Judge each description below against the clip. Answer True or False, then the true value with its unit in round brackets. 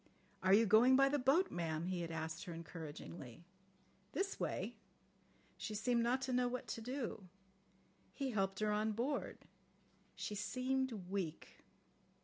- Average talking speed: True (145 wpm)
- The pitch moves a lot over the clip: True (6.5 semitones)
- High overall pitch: True (215 Hz)